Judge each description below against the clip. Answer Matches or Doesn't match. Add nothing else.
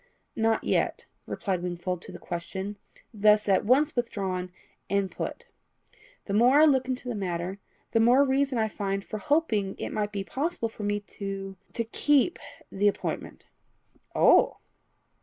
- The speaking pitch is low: Doesn't match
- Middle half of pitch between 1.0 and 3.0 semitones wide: Doesn't match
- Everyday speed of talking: Matches